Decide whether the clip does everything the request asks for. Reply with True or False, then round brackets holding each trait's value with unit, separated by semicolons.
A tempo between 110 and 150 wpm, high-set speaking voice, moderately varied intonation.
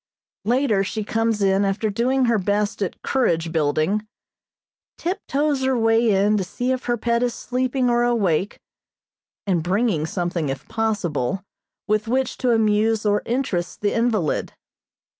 True (145 wpm; 215 Hz; 3.8 semitones)